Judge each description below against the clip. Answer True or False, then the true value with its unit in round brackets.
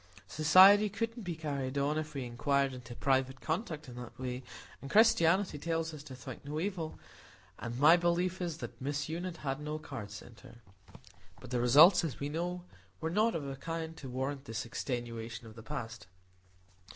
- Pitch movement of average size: True (4.5 semitones)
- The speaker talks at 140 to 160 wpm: False (175 wpm)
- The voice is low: False (145 Hz)